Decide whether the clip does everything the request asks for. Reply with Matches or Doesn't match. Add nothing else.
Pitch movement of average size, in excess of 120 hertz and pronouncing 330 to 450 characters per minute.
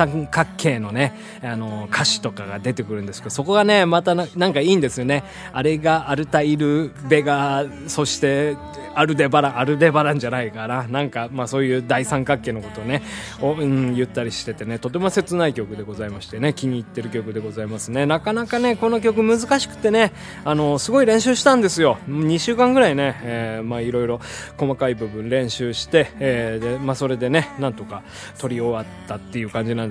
Matches